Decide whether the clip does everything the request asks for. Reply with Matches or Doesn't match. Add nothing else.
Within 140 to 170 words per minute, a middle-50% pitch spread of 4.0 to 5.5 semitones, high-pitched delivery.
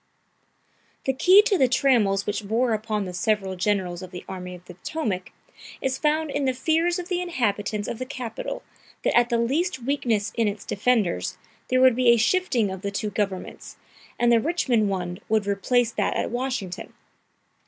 Doesn't match